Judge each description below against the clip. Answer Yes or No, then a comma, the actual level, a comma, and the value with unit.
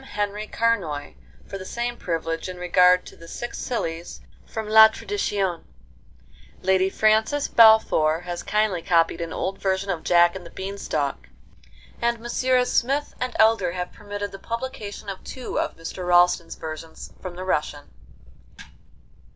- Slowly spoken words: No, average, 145 wpm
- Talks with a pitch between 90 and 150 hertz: No, high, 190 Hz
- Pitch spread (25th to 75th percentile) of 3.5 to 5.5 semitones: Yes, average, 4.2 semitones